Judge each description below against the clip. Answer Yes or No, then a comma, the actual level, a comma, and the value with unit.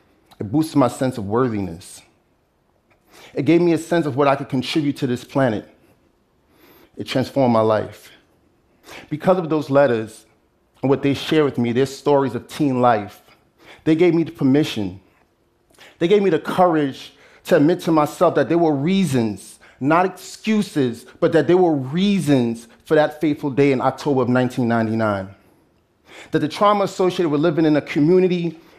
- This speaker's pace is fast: Yes, fast, 165 wpm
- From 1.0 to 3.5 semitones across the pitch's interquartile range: No, average, 5.1 semitones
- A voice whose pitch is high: No, medium, 140 Hz